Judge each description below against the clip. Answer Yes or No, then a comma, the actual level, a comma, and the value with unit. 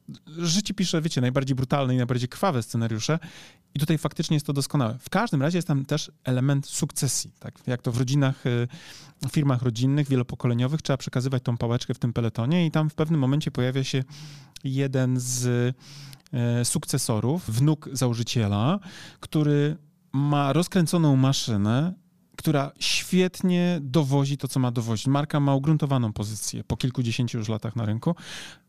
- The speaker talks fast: No, average, 150 wpm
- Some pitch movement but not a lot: Yes, average, 3.7 semitones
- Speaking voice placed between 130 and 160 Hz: Yes, medium, 140 Hz